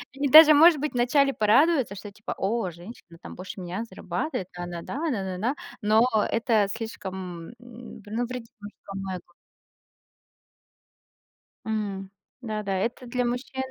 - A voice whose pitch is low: No, high, 220 Hz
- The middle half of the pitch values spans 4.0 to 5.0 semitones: Yes, average, 4.3 semitones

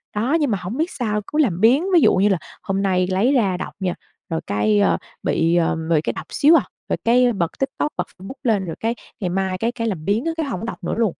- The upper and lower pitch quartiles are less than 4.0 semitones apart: No, wide, 5.4 semitones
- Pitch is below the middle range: No, high, 205 Hz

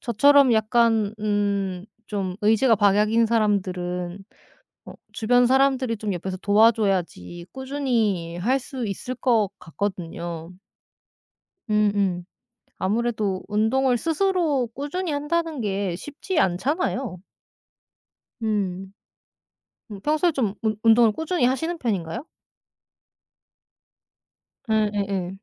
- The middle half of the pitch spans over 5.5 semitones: No, average, 5.2 semitones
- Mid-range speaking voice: No, high, 215 Hz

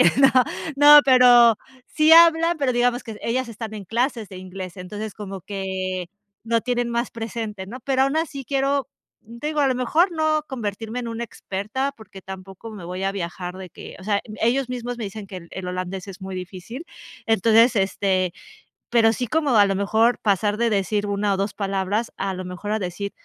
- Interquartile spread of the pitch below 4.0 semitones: No, average, 4.3 semitones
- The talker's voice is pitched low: No, high, 220 Hz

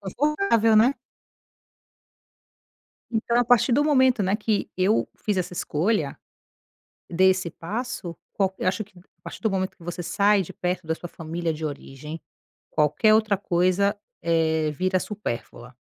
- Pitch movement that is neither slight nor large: Yes, average, 4.6 semitones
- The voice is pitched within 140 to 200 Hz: Yes, high, 190 Hz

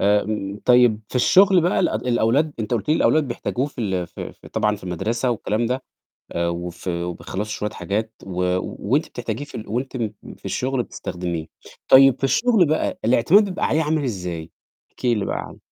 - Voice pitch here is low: Yes, low, 115 Hz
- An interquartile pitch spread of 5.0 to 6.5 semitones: Yes, wide, 5.6 semitones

